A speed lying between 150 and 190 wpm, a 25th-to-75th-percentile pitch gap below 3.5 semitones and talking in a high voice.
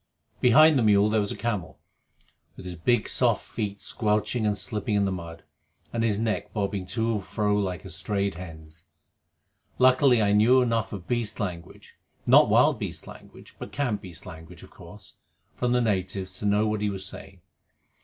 No: average, 185 wpm; average, 3.1 semitones; low, 105 Hz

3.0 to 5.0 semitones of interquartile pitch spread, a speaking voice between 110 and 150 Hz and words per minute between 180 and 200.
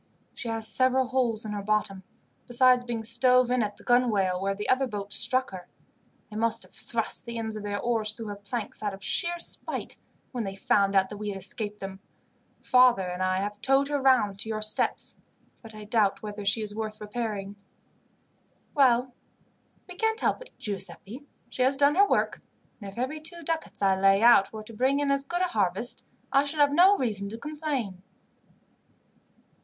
No: average, 4.2 semitones; high, 225 Hz; average, 195 wpm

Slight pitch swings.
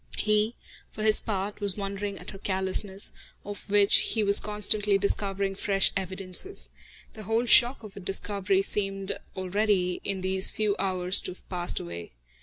Yes: narrow, 1.6 semitones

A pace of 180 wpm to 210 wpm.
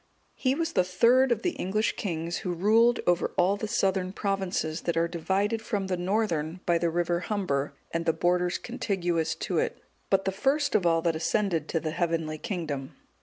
Yes: average, 190 wpm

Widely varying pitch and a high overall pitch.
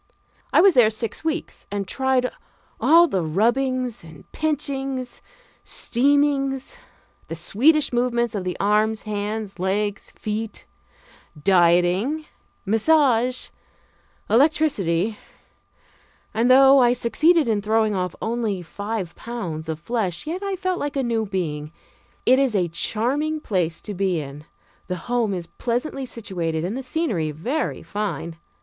Yes: wide, 6.0 semitones; high, 225 Hz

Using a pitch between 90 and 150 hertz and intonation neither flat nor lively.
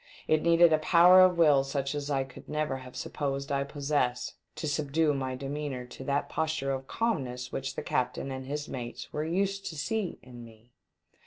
Yes: medium, 140 Hz; average, 3.0 semitones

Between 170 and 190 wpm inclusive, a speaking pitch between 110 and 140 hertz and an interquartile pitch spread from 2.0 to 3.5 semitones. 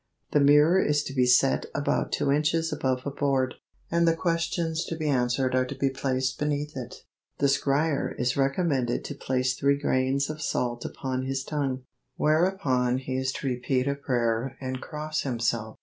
Yes: average, 180 wpm; low, 135 Hz; narrow, 2.5 semitones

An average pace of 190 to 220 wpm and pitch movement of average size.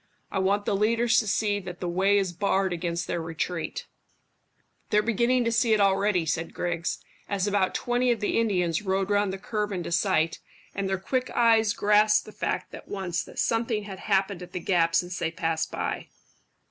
Yes: average, 195 wpm; average, 3.2 semitones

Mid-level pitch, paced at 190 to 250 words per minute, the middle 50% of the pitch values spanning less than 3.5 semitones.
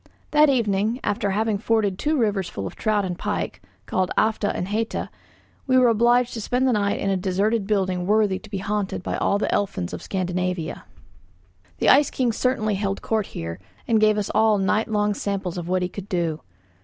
No: high, 205 Hz; average, 200 wpm; average, 2.8 semitones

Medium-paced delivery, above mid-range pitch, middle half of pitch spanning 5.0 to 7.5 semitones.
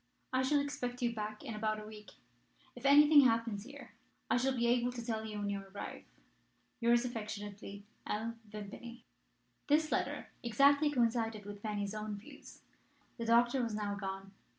No: average, 165 wpm; high, 225 Hz; average, 2.9 semitones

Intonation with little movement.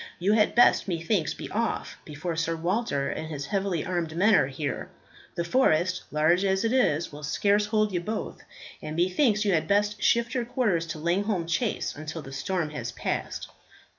No: average, 4.9 semitones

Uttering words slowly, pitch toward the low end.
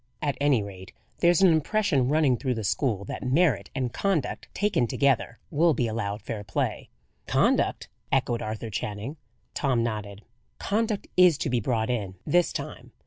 No: average, 160 wpm; low, 125 Hz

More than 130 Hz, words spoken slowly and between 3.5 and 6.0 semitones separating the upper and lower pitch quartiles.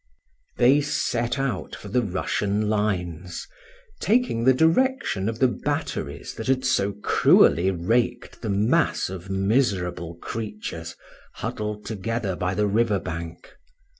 No: low, 105 Hz; slow, 125 wpm; average, 4.2 semitones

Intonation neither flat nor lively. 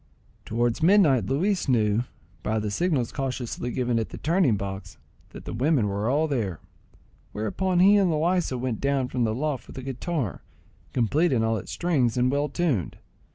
No: wide, 5.9 semitones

